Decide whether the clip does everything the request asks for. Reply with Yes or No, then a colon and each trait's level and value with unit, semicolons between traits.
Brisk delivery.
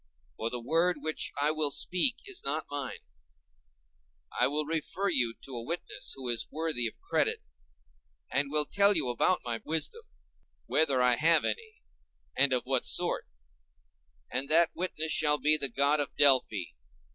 No: average, 155 wpm